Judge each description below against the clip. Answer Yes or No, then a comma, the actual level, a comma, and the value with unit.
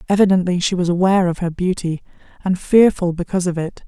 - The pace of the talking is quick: No, average, 185 wpm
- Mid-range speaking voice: Yes, medium, 180 Hz